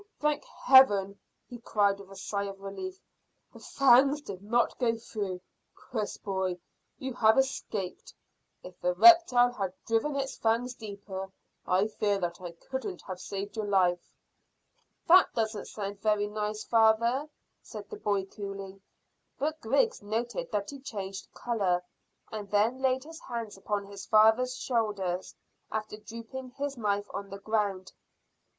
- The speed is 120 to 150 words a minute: Yes, average, 145 wpm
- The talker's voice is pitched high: Yes, high, 215 Hz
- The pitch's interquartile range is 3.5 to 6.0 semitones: Yes, average, 3.8 semitones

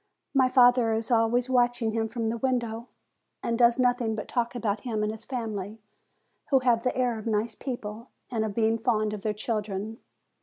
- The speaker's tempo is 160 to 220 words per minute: Yes, average, 190 wpm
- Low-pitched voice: No, high, 230 Hz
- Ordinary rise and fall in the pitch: No, narrow, 2.0 semitones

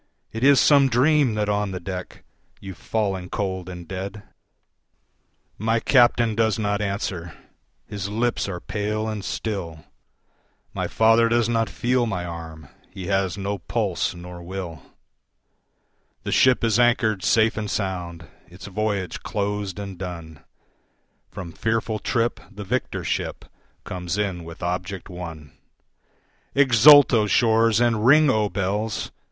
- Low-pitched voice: Yes, low, 105 Hz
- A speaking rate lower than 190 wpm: Yes, average, 140 wpm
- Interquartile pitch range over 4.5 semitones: No, average, 3.7 semitones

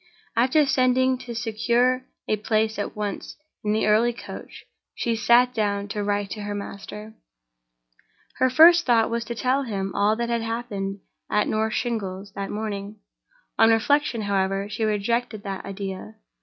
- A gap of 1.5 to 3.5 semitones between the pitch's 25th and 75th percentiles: Yes, average, 2.9 semitones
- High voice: Yes, high, 220 Hz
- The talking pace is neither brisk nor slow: Yes, average, 155 wpm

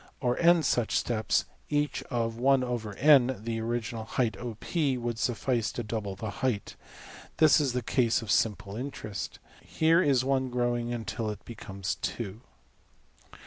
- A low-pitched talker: Yes, low, 120 Hz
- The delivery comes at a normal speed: No, slow, 125 wpm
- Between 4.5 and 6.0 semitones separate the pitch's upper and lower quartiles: No, average, 2.9 semitones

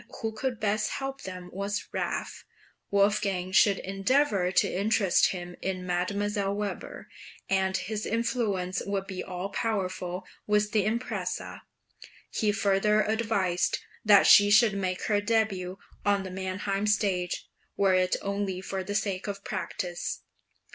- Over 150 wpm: No, average, 140 wpm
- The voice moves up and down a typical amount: No, narrow, 2.2 semitones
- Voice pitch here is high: Yes, high, 200 Hz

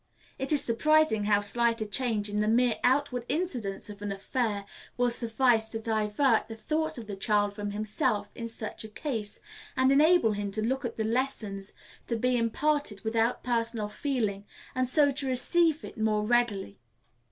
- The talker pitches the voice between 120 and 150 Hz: No, high, 230 Hz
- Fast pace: No, average, 175 wpm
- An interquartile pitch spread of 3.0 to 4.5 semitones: Yes, average, 3.6 semitones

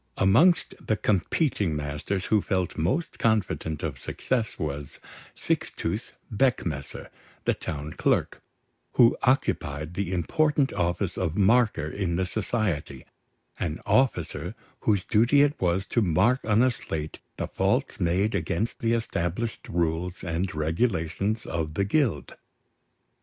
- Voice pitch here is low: Yes, very low, 95 Hz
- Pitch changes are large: Yes, wide, 5.8 semitones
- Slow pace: Yes, slow, 125 wpm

